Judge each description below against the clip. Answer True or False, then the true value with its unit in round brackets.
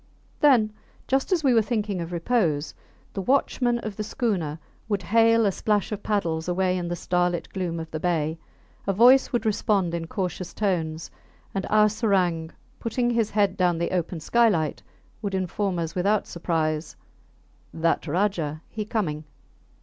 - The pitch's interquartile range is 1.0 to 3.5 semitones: False (4.3 semitones)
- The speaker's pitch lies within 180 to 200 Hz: True (190 Hz)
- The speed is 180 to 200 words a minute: False (160 wpm)